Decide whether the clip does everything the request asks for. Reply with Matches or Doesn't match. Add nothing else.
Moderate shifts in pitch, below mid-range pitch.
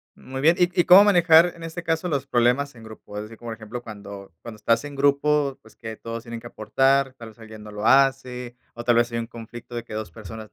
Matches